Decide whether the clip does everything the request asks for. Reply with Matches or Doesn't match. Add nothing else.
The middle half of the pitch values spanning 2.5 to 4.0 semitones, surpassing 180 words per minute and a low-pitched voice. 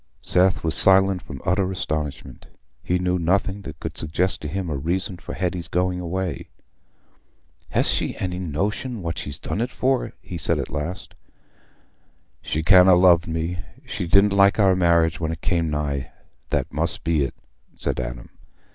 Doesn't match